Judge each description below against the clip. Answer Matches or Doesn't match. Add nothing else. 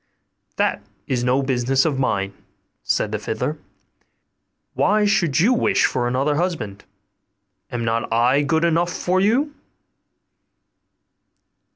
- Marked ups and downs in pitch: Matches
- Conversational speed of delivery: Doesn't match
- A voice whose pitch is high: Doesn't match